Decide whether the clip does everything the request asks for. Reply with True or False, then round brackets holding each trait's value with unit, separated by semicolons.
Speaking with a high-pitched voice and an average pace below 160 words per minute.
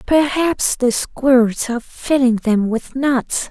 True (255 Hz; 135 wpm)